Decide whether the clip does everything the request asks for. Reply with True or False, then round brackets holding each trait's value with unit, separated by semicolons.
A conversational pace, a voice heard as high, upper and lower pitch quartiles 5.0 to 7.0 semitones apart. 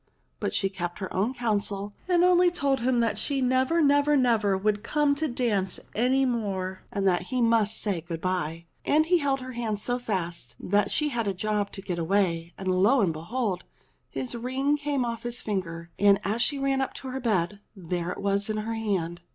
False (210 wpm; 215 Hz; 5.4 semitones)